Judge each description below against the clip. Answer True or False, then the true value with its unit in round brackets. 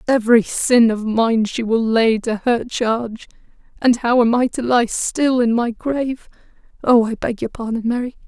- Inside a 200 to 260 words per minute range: False (180 wpm)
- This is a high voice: True (235 Hz)